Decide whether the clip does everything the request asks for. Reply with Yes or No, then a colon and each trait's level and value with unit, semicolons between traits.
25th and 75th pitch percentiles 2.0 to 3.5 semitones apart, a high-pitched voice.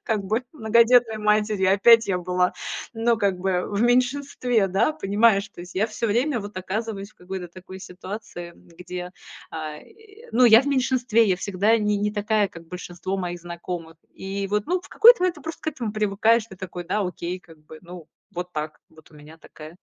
No: average, 4.2 semitones; high, 200 Hz